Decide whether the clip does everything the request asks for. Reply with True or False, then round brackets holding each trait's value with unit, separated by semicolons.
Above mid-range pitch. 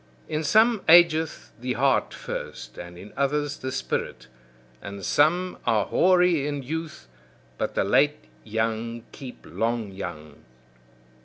False (135 Hz)